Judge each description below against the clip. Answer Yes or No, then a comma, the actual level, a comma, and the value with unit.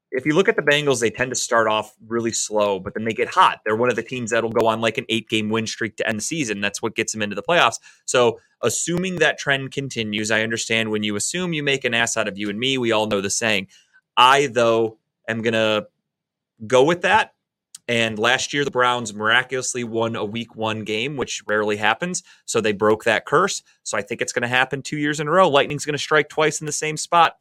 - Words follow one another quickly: Yes, fast, 250 wpm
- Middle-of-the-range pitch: No, low, 115 Hz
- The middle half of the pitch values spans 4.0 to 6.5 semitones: Yes, average, 4.6 semitones